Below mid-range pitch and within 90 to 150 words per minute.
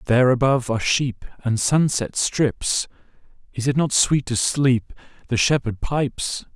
Yes: low, 125 Hz; average, 145 wpm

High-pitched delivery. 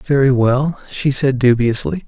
No: low, 130 Hz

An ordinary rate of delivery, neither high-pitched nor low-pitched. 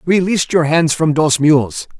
Yes: average, 180 wpm; medium, 155 Hz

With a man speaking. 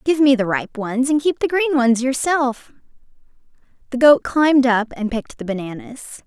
No: female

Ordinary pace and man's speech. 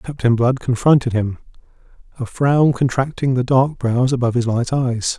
Yes: average, 160 wpm; male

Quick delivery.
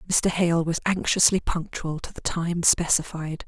No: average, 155 wpm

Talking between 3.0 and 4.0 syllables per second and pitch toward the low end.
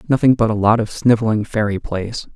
No: 5.6 syllables/s; low, 110 Hz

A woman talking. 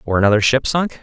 No: male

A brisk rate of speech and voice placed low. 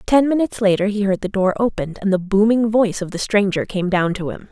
No: fast, 255 wpm; high, 205 Hz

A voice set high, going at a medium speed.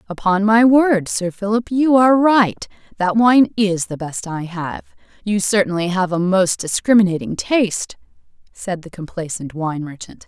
Yes: high, 200 Hz; average, 145 wpm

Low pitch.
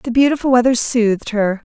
No: high, 235 Hz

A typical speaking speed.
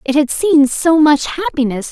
Yes: average, 190 wpm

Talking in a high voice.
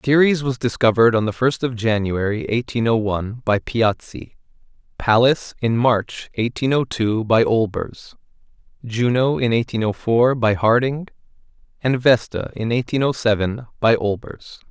No: low, 115 Hz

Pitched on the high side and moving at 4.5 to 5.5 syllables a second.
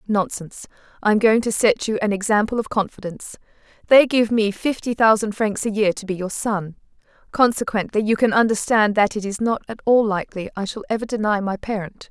No: high, 215 Hz; 5.7 syllables/s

